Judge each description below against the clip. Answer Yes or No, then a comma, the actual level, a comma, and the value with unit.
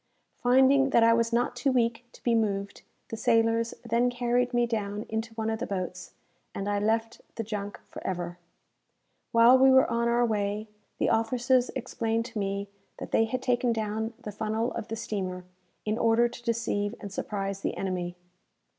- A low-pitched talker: No, high, 225 Hz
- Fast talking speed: No, average, 180 wpm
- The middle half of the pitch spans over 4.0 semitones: No, narrow, 2.5 semitones